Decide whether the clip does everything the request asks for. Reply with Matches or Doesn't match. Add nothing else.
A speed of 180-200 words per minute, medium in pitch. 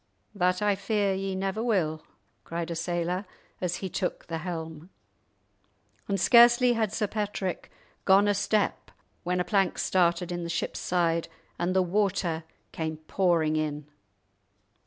Doesn't match